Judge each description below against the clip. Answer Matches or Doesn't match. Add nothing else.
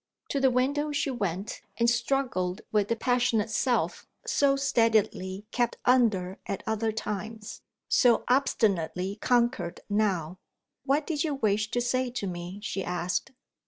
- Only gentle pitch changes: Doesn't match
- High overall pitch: Matches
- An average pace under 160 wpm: Matches